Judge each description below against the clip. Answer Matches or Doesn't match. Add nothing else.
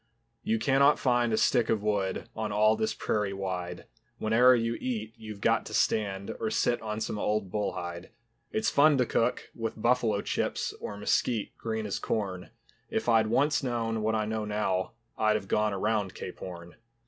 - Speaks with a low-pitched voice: Matches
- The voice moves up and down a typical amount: Doesn't match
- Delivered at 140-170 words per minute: Doesn't match